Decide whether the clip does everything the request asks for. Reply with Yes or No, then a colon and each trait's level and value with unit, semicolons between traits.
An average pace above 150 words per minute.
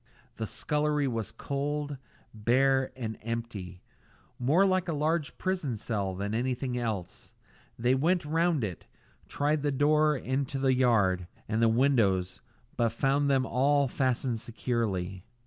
No: slow, 135 wpm